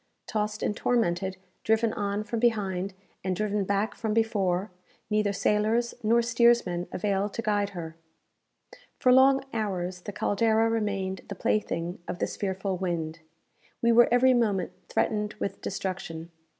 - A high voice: Yes, high, 205 Hz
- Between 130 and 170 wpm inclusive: Yes, average, 140 wpm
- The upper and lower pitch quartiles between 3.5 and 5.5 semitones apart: No, average, 3.0 semitones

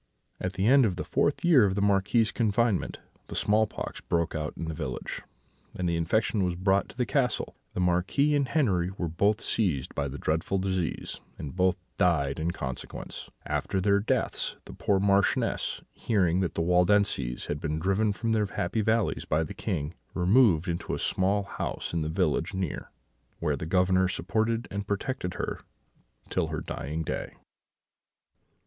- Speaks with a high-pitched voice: No, very low, 95 Hz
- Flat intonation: No, average, 4.0 semitones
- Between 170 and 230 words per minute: Yes, average, 175 wpm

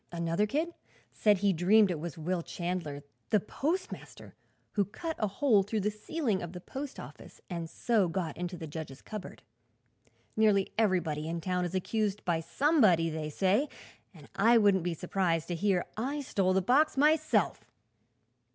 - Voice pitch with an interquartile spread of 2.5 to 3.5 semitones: No, average, 4.4 semitones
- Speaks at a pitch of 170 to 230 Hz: Yes, high, 190 Hz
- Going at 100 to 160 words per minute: No, average, 170 wpm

